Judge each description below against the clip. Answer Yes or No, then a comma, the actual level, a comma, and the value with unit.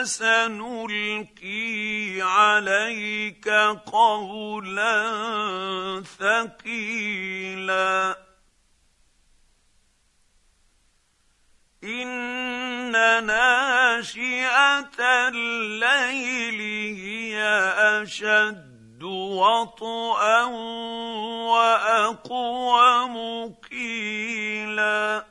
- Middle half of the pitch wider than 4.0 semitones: No, narrow, 2.6 semitones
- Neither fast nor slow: No, slow, 30 wpm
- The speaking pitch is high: Yes, high, 215 Hz